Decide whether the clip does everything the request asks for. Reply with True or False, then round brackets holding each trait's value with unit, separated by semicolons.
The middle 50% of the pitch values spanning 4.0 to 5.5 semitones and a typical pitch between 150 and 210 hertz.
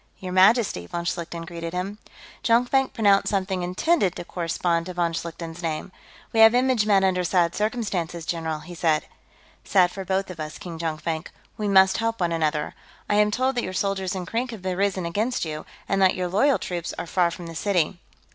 False (3.4 semitones; 185 Hz)